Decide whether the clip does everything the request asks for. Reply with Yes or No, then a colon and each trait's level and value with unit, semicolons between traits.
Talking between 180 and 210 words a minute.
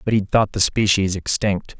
Yes: average, 200 wpm